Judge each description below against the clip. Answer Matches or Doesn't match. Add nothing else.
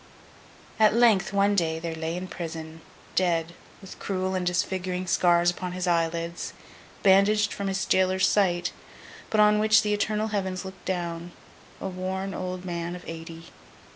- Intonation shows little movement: Matches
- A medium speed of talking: Matches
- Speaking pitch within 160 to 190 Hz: Matches